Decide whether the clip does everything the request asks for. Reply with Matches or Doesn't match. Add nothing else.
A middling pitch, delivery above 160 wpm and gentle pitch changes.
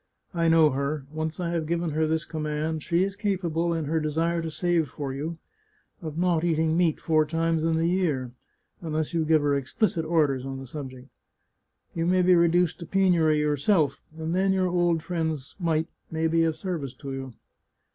Matches